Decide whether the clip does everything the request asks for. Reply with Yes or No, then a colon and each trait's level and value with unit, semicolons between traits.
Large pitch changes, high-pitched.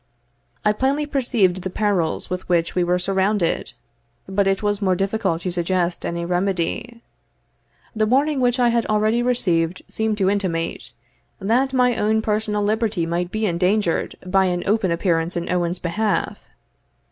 No: average, 3.7 semitones; high, 195 Hz